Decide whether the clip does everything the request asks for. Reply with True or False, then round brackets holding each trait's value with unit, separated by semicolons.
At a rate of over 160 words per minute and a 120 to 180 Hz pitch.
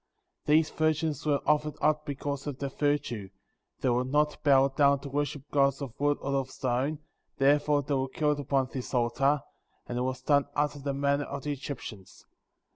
True (190 wpm; 140 Hz)